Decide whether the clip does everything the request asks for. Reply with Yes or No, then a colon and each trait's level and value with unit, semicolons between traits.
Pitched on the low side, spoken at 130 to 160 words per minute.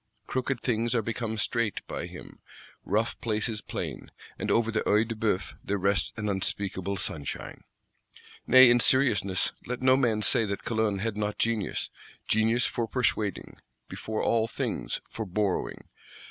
Yes: low, 110 Hz; average, 150 wpm